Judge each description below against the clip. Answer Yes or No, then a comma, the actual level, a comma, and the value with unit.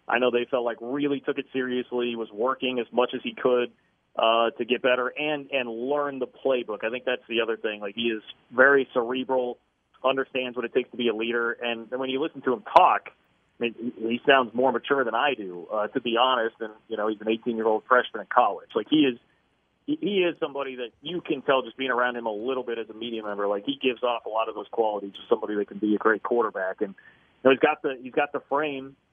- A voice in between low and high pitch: No, low, 125 Hz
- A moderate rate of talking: No, fast, 260 wpm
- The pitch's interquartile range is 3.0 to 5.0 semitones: No, narrow, 2.6 semitones